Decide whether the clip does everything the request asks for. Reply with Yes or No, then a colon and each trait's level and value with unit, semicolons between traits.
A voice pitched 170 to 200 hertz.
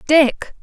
No: very high, 295 Hz